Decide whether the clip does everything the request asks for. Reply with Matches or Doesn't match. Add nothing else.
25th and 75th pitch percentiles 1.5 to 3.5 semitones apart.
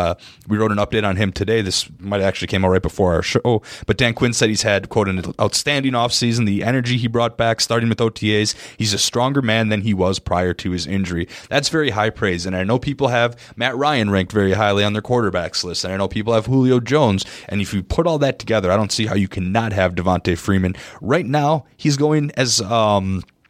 Doesn't match